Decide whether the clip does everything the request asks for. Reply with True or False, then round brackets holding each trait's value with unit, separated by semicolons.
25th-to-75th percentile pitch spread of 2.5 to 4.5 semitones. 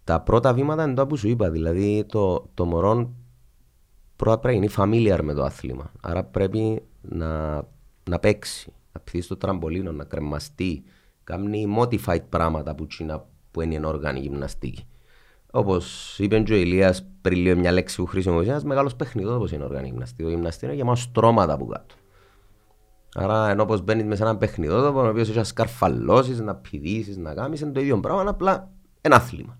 False (5.3 semitones)